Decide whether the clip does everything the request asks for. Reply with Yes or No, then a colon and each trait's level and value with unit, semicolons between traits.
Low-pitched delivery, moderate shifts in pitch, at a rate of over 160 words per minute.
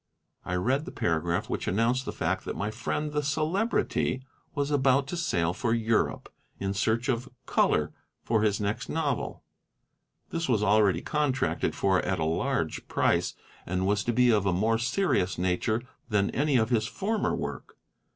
No: low, 115 Hz; wide, 5.9 semitones; average, 170 wpm